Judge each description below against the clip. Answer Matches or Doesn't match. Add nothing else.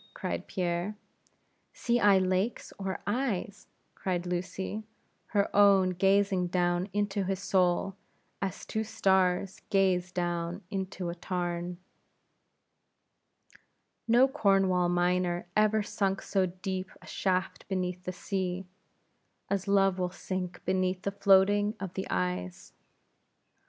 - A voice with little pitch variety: Matches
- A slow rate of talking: Matches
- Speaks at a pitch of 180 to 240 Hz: Matches